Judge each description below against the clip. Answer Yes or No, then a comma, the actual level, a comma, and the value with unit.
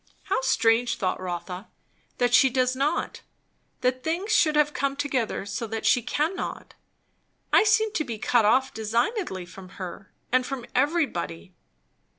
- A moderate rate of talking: Yes, average, 150 wpm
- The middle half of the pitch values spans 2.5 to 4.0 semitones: No, average, 5.2 semitones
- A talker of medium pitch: No, very high, 250 Hz